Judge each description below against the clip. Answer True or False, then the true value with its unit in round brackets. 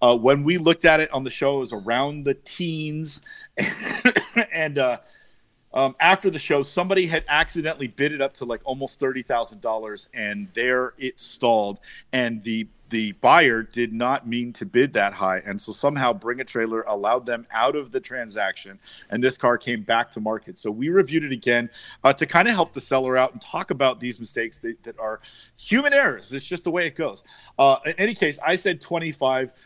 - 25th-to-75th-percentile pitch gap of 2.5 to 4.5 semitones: False (5.3 semitones)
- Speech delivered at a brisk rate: True (210 wpm)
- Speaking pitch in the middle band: False (130 Hz)